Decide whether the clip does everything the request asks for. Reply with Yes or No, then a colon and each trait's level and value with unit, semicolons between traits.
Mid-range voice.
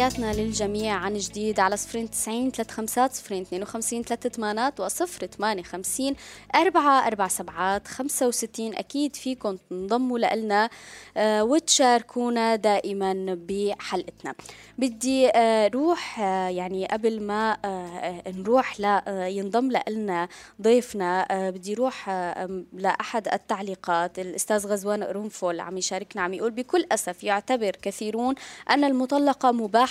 No: high, 215 Hz